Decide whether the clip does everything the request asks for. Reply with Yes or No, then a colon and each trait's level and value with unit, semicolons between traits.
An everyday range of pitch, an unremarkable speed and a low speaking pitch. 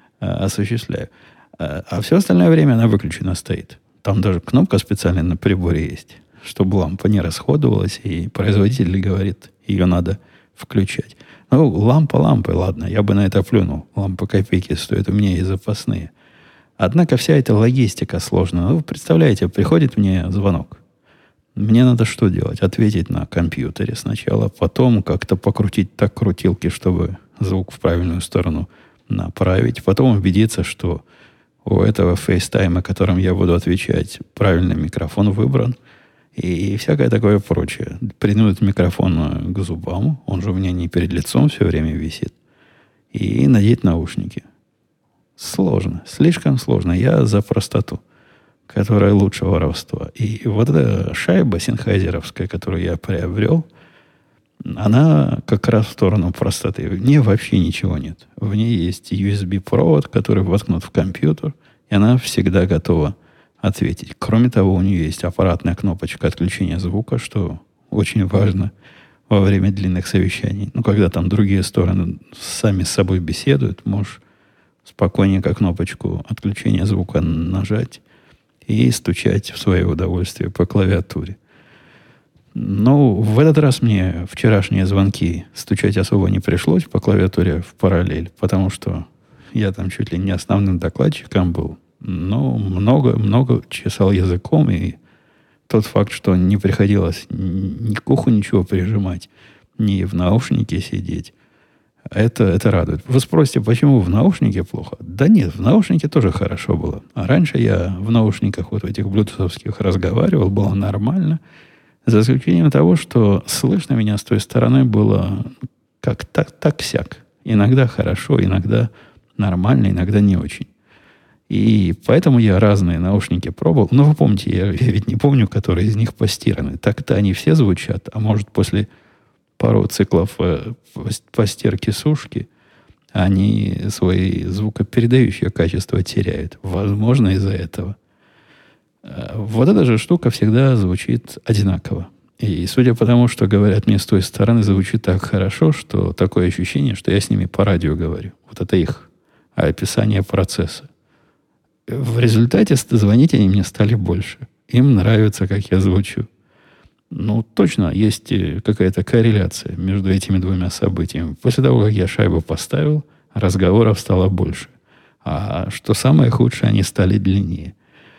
Yes: average, 3.6 semitones; average, 140 wpm; low, 100 Hz